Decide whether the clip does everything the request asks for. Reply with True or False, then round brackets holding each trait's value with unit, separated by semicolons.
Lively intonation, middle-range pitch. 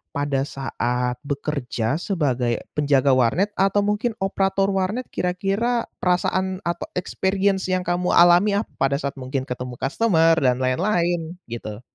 True (6.3 semitones; 170 Hz)